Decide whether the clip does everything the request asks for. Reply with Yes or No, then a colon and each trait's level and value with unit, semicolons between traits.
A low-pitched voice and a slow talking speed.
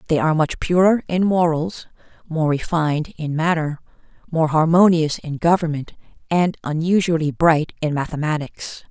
No: medium, 160 Hz; slow, 130 wpm